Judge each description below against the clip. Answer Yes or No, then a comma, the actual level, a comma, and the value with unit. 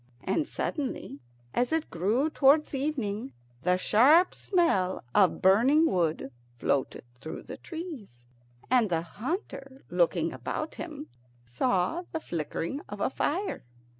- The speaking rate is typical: No, slow, 125 wpm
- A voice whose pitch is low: No, high, 235 Hz